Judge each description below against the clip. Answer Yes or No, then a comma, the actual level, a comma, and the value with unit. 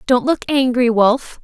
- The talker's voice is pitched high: Yes, very high, 250 Hz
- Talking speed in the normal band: Yes, average, 165 wpm